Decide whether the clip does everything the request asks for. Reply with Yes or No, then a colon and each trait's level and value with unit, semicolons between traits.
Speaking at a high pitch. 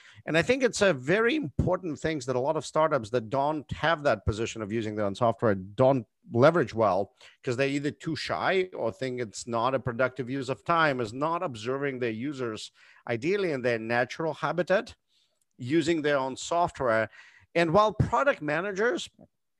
No: low, 135 Hz